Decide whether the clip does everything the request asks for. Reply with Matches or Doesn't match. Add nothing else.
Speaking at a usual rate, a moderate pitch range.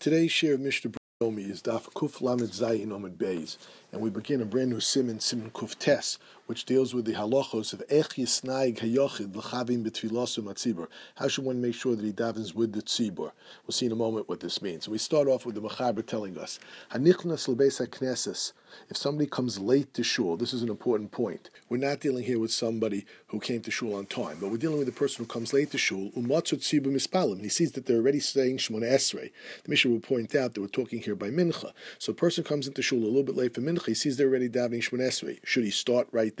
Doesn't match